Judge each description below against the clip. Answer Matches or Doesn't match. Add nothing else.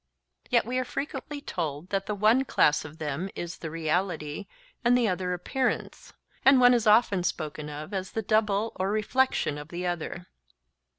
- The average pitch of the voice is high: Matches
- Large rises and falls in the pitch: Matches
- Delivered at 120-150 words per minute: Doesn't match